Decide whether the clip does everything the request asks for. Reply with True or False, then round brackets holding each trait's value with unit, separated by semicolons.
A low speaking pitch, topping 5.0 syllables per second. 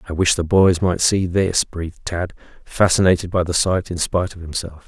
True (90 Hz; 5.3 syllables/s)